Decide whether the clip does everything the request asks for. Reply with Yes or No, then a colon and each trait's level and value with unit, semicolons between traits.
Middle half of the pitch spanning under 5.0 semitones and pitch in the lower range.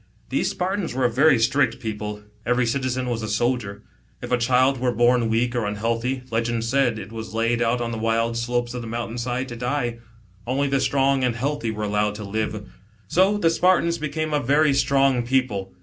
Yes: average, 2.9 semitones; low, 120 Hz